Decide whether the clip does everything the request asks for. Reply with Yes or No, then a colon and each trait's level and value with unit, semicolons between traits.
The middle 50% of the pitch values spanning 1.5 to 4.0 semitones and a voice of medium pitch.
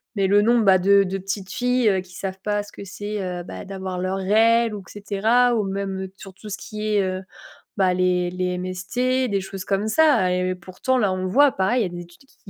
No: narrow, 2.4 semitones; high, 195 Hz